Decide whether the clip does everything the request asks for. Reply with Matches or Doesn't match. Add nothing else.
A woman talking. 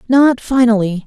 Matches